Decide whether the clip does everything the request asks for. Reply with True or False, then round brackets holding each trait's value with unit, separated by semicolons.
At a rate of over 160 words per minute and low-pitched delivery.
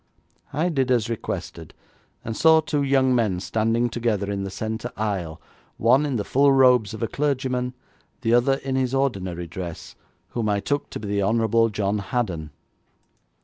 True (170 wpm; 115 Hz)